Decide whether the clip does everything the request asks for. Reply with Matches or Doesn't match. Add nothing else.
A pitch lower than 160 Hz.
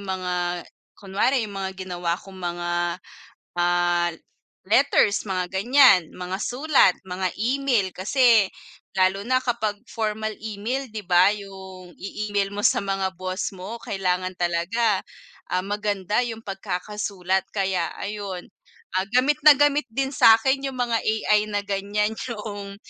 Doesn't match